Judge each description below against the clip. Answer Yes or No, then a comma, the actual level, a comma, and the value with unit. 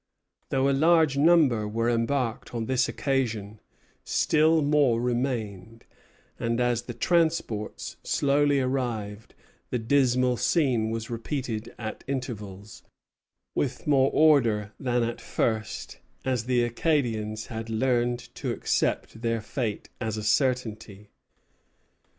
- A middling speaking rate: No, slow, 115 wpm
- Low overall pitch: Yes, low, 120 Hz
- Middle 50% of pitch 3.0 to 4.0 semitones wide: Yes, average, 3.4 semitones